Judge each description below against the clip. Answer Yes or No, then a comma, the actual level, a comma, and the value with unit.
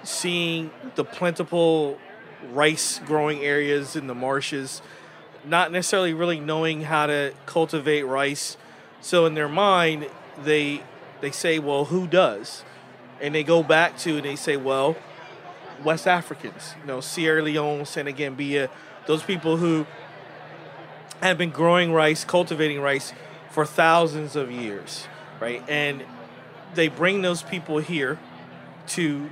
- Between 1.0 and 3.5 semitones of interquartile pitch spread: Yes, average, 2.8 semitones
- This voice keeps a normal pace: No, slow, 130 wpm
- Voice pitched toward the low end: No, medium, 155 Hz